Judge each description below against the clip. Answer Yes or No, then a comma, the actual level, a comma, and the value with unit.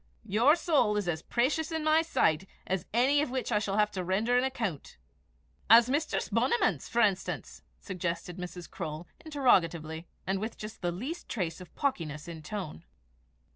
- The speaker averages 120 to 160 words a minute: No, average, 175 wpm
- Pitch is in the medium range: No, high, 210 Hz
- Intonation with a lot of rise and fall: Yes, wide, 6.8 semitones